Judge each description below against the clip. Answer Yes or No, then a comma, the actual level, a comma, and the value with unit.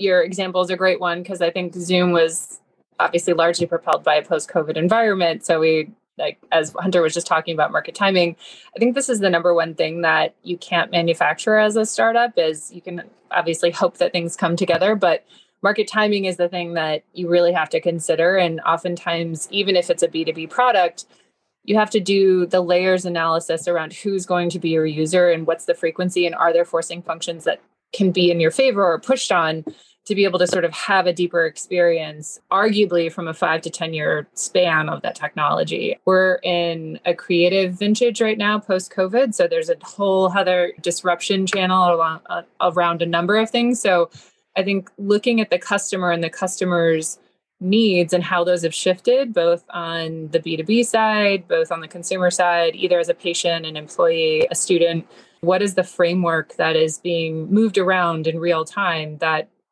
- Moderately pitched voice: Yes, medium, 175 Hz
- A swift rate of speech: No, average, 195 wpm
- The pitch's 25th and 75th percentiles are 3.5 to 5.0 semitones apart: No, average, 2.7 semitones